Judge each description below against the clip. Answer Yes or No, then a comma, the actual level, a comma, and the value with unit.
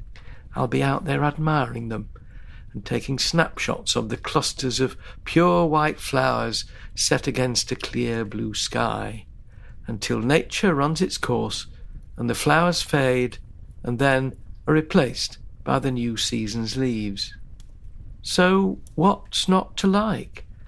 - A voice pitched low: Yes, low, 120 Hz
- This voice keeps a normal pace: No, slow, 130 wpm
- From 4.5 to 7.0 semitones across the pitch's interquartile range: Yes, average, 5.1 semitones